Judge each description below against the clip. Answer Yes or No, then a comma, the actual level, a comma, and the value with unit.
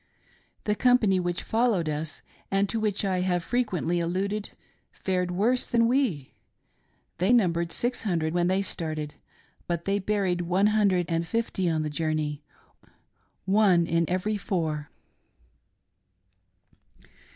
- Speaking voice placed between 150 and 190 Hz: Yes, medium, 185 Hz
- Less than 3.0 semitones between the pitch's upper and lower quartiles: No, average, 3.8 semitones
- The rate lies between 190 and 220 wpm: No, slow, 135 wpm